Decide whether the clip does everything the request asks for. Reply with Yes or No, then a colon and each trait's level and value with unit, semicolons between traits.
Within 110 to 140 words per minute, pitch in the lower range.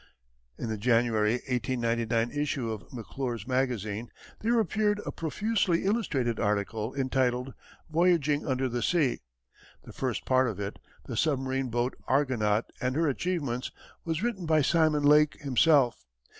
Yes: slow, 135 wpm; low, 130 Hz